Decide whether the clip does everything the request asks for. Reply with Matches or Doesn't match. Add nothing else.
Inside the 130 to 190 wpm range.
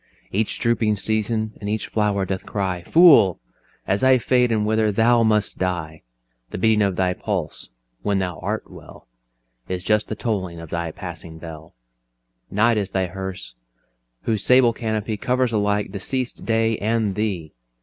Matches